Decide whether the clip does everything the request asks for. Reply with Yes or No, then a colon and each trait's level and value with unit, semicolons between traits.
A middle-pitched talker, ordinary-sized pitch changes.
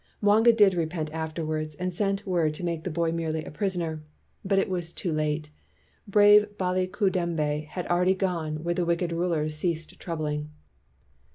Yes: medium, 170 Hz; average, 3.0 semitones